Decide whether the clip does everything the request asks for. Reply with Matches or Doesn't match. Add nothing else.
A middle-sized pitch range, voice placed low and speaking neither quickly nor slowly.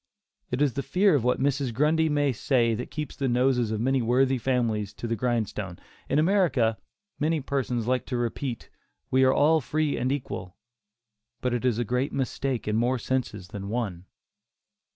Matches